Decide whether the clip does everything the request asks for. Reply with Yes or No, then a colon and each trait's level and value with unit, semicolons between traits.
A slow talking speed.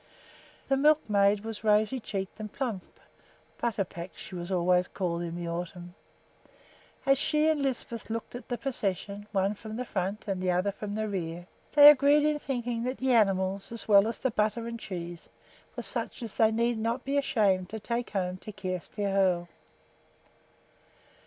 No: average, 170 wpm